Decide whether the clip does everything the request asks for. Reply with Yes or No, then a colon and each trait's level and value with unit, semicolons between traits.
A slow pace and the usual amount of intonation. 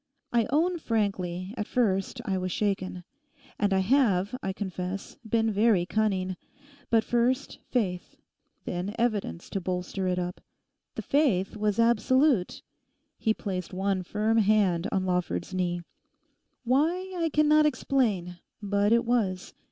Yes: slow, 130 wpm; average, 4.3 semitones